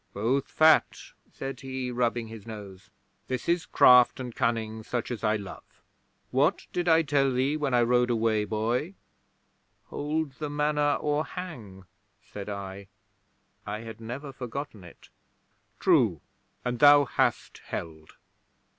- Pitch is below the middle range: Yes, low, 125 Hz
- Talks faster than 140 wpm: No, slow, 135 wpm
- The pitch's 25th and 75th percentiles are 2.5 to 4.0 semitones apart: No, average, 4.8 semitones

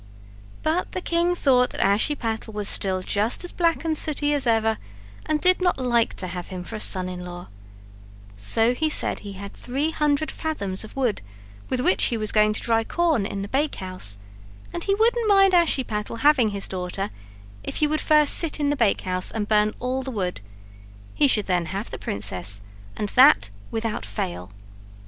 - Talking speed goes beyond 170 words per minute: Yes, average, 185 wpm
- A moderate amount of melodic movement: No, wide, 7.4 semitones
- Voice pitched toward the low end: No, high, 225 Hz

